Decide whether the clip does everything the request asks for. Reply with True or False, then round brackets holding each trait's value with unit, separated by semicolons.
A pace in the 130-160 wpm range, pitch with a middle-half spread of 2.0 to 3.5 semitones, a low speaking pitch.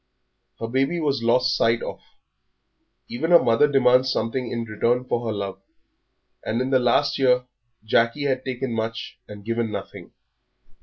True (155 wpm; 2.4 semitones; 120 Hz)